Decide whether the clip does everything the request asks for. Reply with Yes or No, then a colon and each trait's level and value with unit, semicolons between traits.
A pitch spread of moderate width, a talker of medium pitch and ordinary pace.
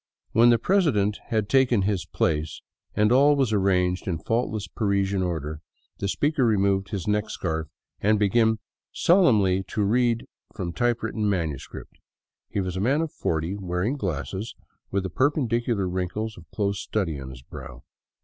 No: average, 4.2 semitones; low, 100 Hz; average, 160 wpm